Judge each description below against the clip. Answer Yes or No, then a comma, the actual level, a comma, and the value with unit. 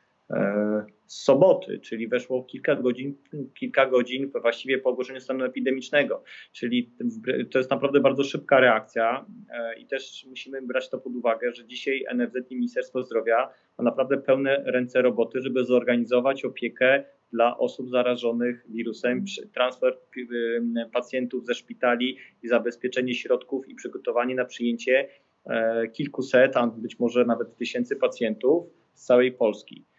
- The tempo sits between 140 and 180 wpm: No, average, 130 wpm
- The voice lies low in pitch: Yes, low, 125 Hz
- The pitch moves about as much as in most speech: No, narrow, 1.9 semitones